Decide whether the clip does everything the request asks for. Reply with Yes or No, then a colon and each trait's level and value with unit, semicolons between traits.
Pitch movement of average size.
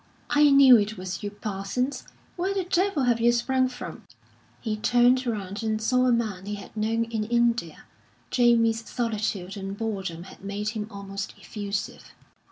Yes: average, 3.4 semitones